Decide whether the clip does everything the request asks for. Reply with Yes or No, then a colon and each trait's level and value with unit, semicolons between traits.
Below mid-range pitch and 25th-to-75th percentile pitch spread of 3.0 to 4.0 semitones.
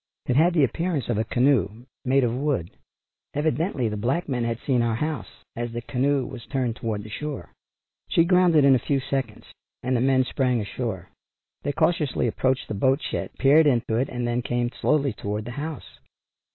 Yes: low, 130 Hz; average, 3.4 semitones